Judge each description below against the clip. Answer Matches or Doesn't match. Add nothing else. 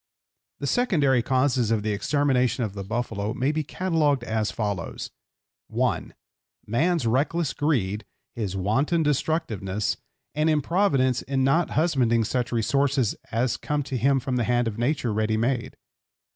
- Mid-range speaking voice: Doesn't match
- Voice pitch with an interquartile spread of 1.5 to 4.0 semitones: Doesn't match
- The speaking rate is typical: Matches